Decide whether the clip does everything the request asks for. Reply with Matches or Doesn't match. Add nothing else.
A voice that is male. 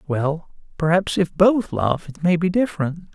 Matches